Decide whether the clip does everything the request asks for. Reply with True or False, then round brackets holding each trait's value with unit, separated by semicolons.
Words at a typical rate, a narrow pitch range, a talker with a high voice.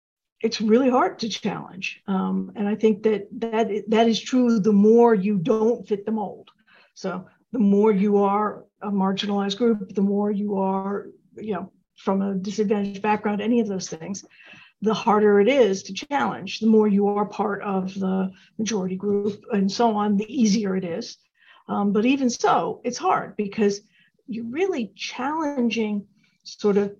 True (170 wpm; 2.0 semitones; 210 Hz)